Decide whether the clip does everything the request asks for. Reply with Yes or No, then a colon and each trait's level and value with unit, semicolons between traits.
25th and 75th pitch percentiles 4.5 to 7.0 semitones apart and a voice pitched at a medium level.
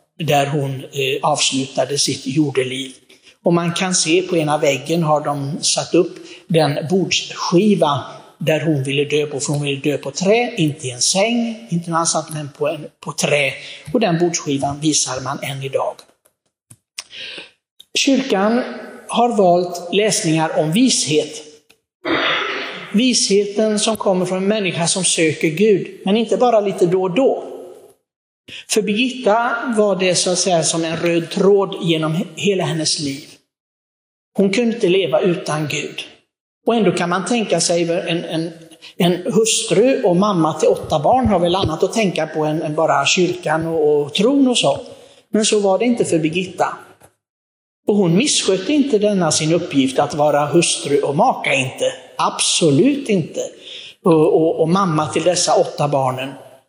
Yes: average, 5.2 semitones; medium, 170 Hz